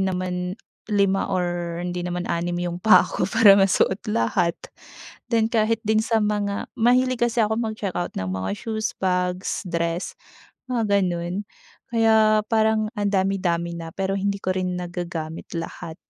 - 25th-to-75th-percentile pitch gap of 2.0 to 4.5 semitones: Yes, average, 3.7 semitones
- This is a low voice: No, high, 190 Hz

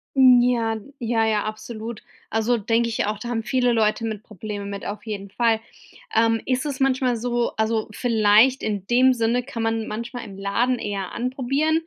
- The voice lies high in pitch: Yes, high, 230 Hz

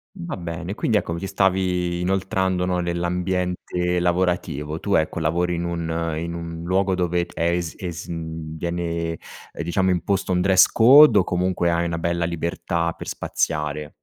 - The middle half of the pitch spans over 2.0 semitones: No, narrow, 1.6 semitones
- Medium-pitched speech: No, very low, 85 Hz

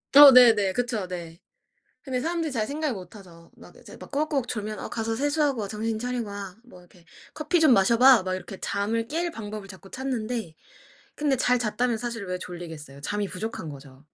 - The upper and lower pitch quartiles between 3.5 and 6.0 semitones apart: Yes, average, 5.1 semitones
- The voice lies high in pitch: Yes, high, 220 Hz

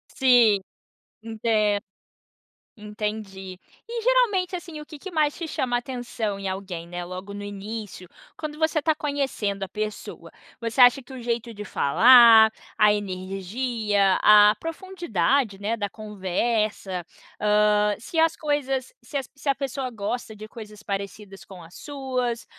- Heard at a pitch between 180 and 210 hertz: No, high, 220 Hz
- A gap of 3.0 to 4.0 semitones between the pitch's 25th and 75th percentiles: No, average, 4.8 semitones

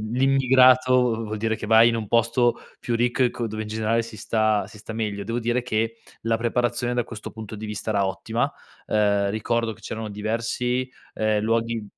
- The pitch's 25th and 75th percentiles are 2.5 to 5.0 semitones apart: No, narrow, 1.8 semitones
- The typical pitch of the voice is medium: No, low, 115 Hz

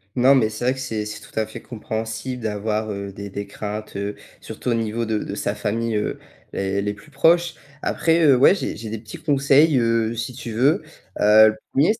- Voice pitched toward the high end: No, low, 110 Hz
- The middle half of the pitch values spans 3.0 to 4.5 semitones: Yes, average, 3.7 semitones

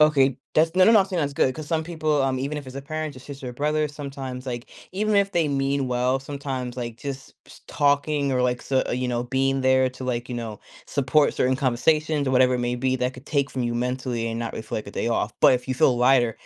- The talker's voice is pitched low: Yes, low, 130 Hz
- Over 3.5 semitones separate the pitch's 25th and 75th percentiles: No, average, 2.7 semitones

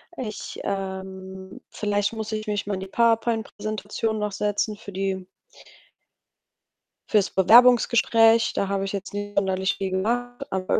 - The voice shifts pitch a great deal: No, narrow, 2.5 semitones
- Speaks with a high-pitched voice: Yes, high, 205 Hz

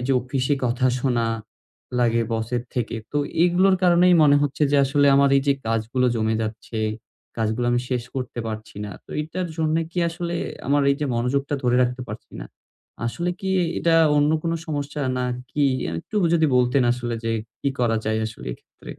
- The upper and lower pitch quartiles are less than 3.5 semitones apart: No, average, 3.8 semitones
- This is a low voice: Yes, low, 130 Hz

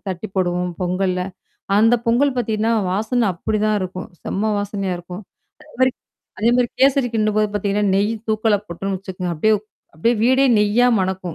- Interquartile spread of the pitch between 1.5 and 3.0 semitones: No, average, 3.5 semitones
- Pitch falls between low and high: No, high, 210 Hz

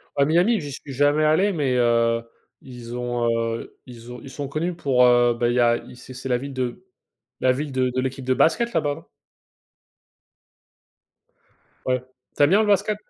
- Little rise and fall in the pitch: No, average, 3.5 semitones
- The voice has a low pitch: Yes, low, 130 Hz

